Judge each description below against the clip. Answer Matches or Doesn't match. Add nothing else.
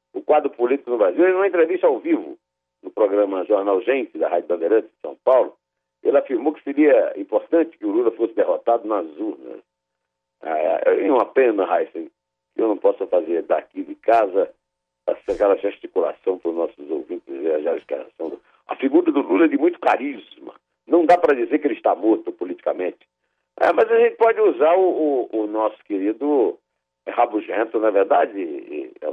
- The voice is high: Matches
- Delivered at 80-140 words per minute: Doesn't match